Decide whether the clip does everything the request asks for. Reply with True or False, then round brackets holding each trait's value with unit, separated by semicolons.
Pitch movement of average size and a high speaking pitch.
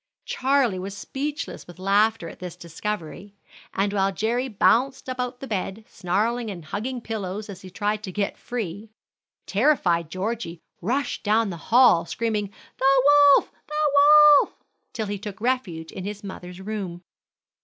True (4.9 semitones; 210 Hz)